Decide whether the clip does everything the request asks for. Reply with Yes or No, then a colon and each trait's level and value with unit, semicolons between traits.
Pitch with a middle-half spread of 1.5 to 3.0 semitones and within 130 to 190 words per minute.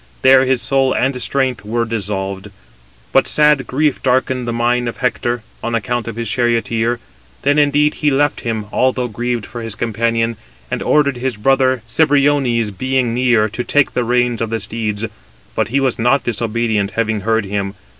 Yes: narrow, 2.6 semitones; average, 175 wpm